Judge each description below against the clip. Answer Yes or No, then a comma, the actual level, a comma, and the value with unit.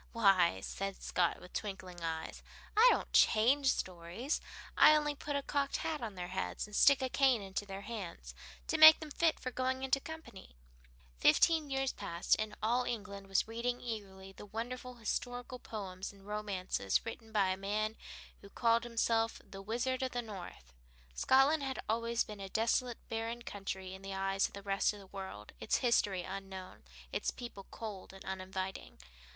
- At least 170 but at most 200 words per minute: Yes, average, 175 wpm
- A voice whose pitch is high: Yes, high, 215 Hz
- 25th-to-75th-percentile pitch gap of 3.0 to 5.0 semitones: Yes, average, 4.4 semitones